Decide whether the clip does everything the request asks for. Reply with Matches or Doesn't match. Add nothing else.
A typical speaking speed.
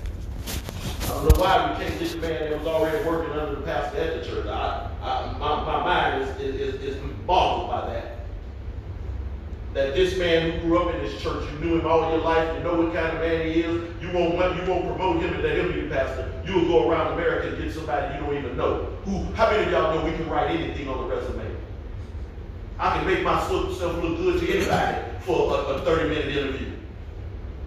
Doesn't match